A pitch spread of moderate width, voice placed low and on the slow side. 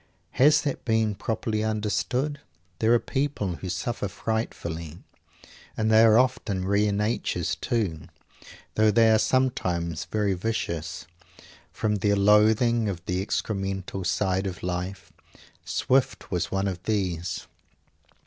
Yes: average, 3.4 semitones; low, 105 Hz; slow, 125 wpm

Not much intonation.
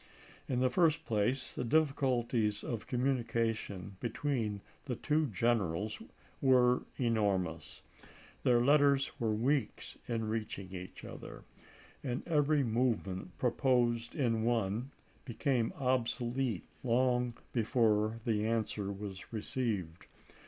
No: average, 3.3 semitones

